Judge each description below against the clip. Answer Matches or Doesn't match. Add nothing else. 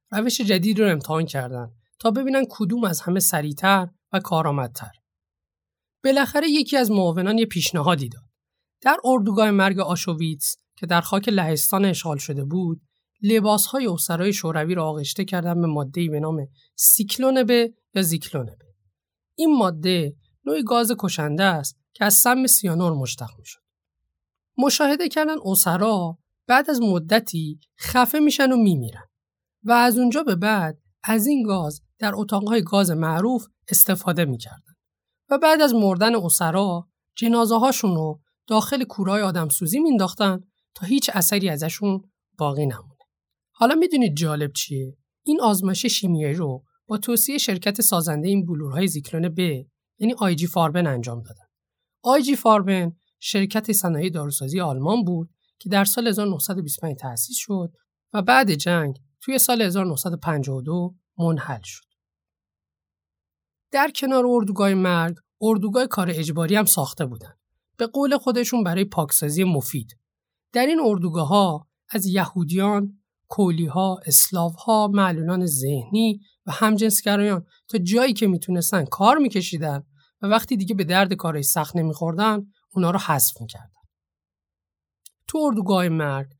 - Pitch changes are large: Matches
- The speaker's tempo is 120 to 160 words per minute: Matches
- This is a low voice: Doesn't match